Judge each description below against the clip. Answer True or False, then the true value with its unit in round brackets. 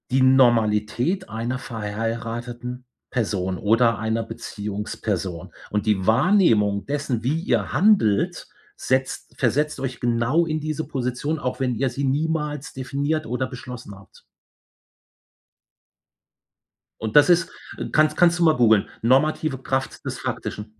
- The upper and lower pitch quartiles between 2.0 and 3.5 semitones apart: False (4.8 semitones)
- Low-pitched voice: True (125 Hz)